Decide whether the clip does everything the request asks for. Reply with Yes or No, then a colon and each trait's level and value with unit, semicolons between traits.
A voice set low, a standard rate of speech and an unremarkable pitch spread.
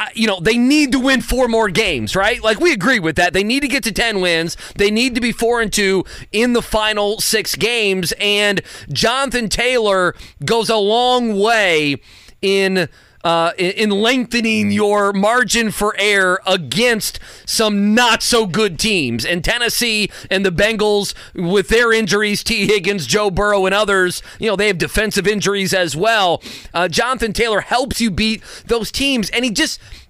No: high, 210 Hz; average, 175 wpm; average, 3.2 semitones